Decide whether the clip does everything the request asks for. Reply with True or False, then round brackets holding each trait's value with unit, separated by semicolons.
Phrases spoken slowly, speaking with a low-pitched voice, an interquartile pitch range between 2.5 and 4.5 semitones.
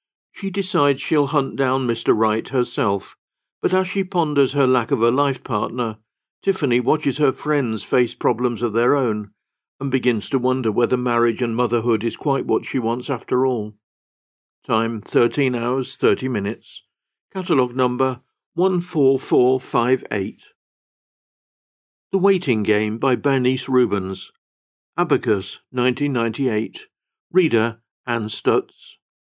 True (125 wpm; 125 Hz; 3.5 semitones)